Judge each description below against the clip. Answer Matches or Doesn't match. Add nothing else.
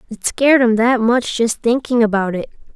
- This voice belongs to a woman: Matches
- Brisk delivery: Doesn't match